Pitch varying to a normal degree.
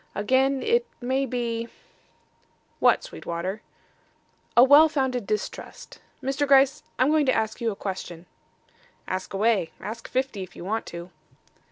Yes: average, 4.9 semitones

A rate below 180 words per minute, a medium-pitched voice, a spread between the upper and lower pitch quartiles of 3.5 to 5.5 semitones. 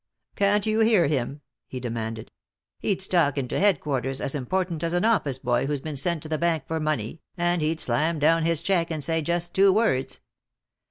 No: average, 195 wpm; medium, 160 Hz; average, 4.2 semitones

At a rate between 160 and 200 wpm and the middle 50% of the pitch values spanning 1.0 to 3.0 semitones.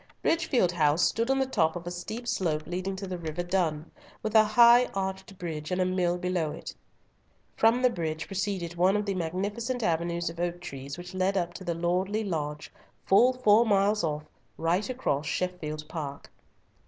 No: average, 185 wpm; average, 3.7 semitones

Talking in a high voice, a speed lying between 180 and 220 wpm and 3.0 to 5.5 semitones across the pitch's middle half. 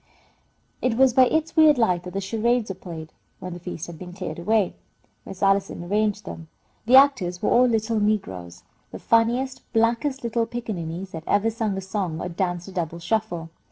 Yes: high, 205 Hz; average, 190 wpm; average, 4.6 semitones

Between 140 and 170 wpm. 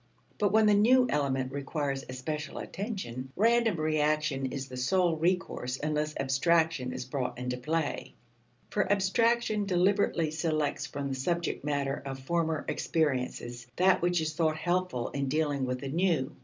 Yes: average, 150 wpm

